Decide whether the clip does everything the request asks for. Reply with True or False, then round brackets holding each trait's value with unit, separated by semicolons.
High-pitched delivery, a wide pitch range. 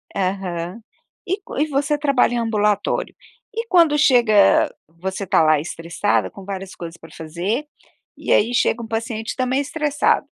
True (220 Hz; 6.7 semitones)